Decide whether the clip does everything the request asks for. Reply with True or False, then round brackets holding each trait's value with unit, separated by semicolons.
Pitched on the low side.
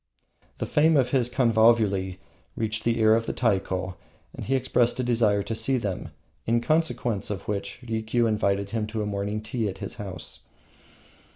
True (110 Hz)